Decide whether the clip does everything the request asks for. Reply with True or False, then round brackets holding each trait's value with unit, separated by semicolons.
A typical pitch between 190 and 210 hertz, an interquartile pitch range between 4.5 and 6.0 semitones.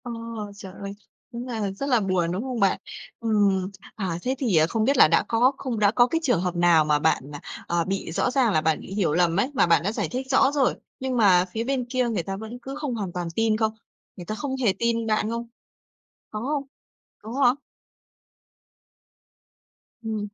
False (220 Hz; 4.9 semitones)